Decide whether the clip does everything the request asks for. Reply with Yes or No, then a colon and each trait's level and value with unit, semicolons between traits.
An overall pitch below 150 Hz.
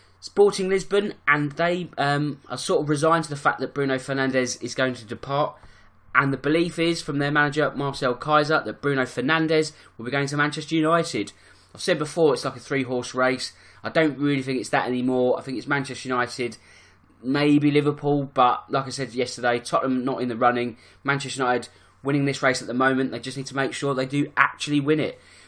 Yes: low, 135 Hz